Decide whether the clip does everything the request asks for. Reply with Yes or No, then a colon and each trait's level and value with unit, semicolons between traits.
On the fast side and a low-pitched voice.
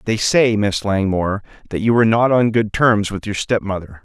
Yes: fast, 210 wpm; low, 105 Hz